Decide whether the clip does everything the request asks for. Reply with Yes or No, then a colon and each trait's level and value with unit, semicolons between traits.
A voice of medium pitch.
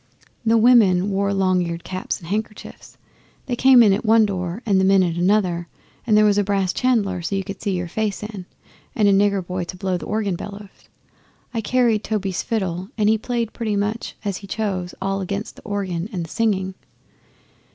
No: high, 200 Hz